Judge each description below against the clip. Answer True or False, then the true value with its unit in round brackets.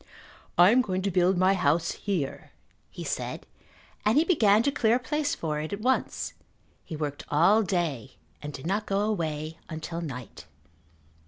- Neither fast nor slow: True (170 wpm)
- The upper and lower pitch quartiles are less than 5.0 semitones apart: False (5.5 semitones)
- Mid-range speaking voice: True (180 Hz)